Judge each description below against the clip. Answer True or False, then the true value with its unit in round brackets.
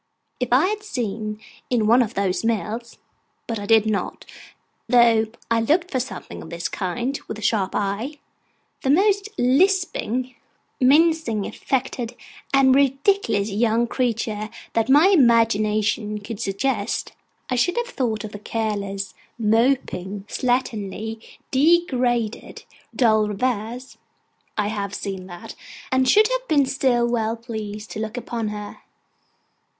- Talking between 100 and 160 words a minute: True (135 wpm)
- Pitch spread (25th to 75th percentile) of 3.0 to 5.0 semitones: True (3.8 semitones)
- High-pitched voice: True (230 Hz)